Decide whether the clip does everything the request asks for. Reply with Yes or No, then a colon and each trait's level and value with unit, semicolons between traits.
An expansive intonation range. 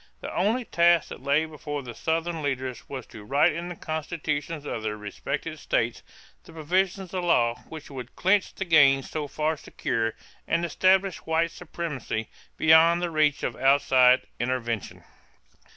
No: average, 4.5 semitones